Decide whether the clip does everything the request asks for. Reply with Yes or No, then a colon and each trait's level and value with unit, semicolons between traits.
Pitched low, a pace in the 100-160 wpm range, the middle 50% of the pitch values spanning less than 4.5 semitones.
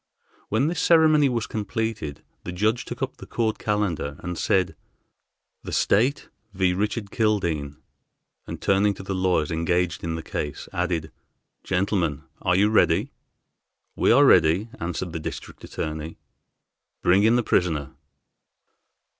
No: very low, 95 Hz; average, 140 wpm; average, 4.9 semitones